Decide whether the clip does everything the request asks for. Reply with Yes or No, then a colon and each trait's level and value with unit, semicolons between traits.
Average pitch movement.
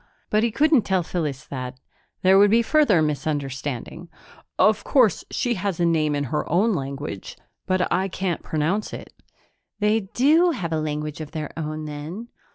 No: wide, 6.0 semitones